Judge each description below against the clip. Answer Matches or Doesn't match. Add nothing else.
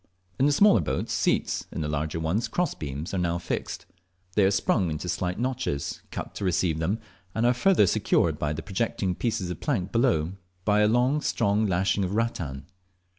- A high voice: Doesn't match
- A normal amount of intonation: Doesn't match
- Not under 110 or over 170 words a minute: Doesn't match